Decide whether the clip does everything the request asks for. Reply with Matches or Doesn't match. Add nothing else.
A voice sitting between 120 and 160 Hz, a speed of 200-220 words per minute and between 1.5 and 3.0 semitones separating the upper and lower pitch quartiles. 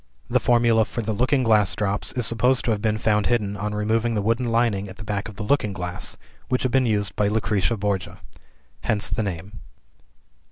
Doesn't match